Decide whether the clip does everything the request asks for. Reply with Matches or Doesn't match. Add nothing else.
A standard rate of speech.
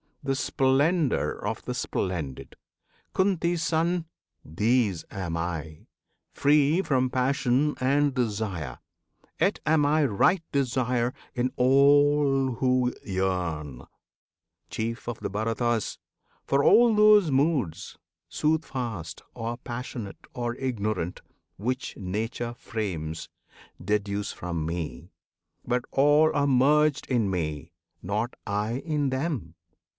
Doesn't match